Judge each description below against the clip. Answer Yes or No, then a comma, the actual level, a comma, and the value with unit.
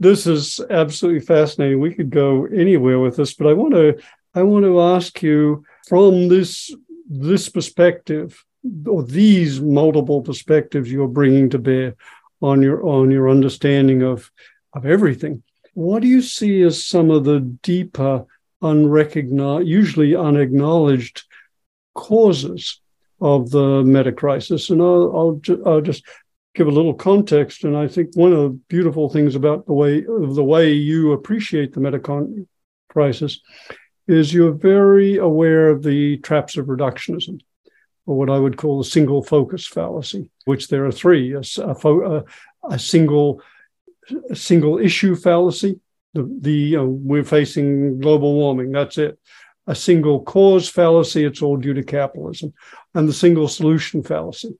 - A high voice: No, medium, 150 Hz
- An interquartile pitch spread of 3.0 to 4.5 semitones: Yes, average, 3.8 semitones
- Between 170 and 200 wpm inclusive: No, average, 155 wpm